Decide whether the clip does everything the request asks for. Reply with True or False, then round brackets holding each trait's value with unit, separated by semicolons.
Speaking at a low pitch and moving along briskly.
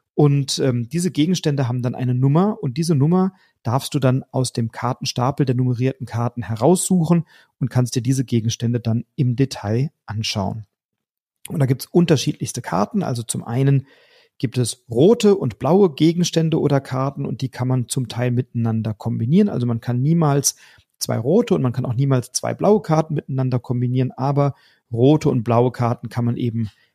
False (130 Hz; 175 wpm)